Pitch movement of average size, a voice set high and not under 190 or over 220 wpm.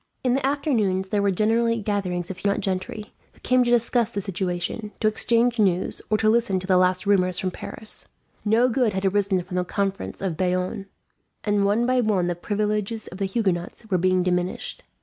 Yes: average, 3.4 semitones; high, 200 Hz; average, 195 wpm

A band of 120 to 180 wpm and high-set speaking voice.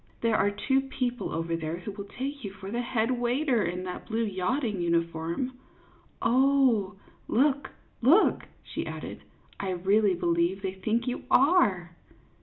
Yes: average, 155 wpm; high, 215 Hz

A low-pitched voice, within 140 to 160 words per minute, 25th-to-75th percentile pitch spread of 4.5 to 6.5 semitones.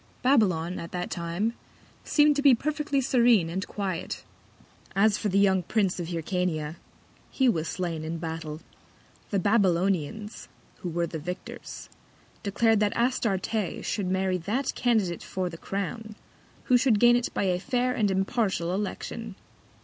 No: high, 195 Hz; average, 150 wpm; average, 4.8 semitones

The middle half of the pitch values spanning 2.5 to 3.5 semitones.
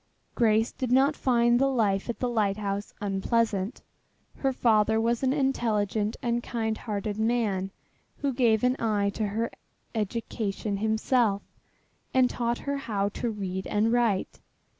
Yes: average, 2.8 semitones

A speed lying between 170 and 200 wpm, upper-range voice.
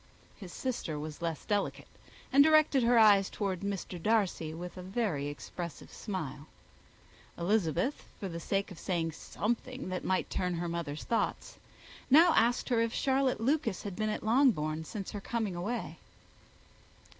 No: average, 155 wpm; high, 200 Hz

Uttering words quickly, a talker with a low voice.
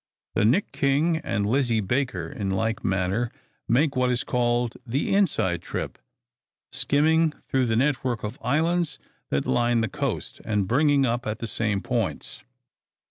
No: average, 150 wpm; low, 120 Hz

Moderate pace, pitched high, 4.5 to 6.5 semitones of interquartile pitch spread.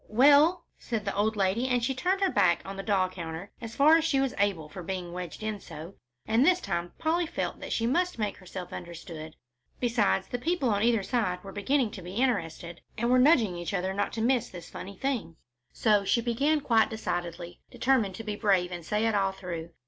No: fast, 215 wpm; high, 210 Hz; wide, 5.6 semitones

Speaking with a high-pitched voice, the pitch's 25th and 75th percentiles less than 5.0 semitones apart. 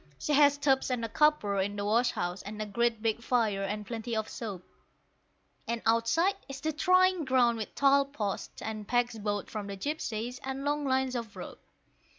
Yes: high, 235 Hz; average, 4.5 semitones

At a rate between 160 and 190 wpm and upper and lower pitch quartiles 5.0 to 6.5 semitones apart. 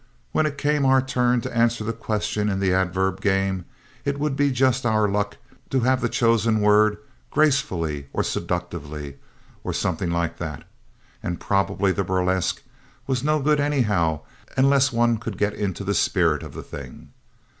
Yes: average, 165 wpm; wide, 5.6 semitones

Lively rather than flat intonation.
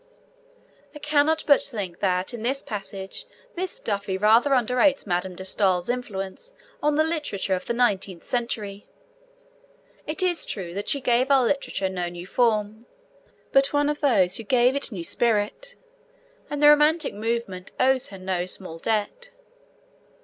Yes: wide, 6.7 semitones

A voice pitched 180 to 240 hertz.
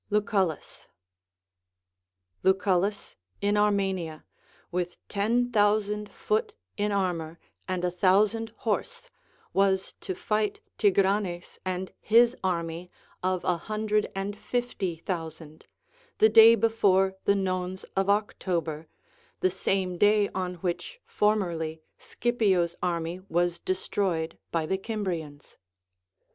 Yes: high, 190 Hz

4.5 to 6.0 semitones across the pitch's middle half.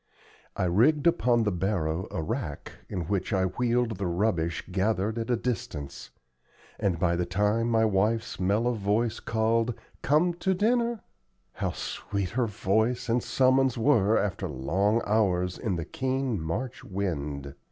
Yes: average, 4.8 semitones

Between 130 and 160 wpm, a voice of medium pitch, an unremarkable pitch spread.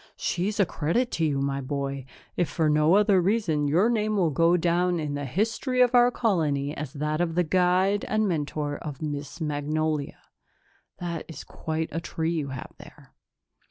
No: average, 175 wpm; medium, 160 Hz; average, 4.2 semitones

